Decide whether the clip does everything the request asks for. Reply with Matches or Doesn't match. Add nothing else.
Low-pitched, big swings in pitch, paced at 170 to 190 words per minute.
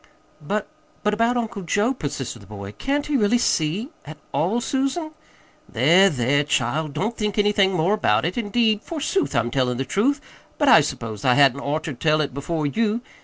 Doesn't match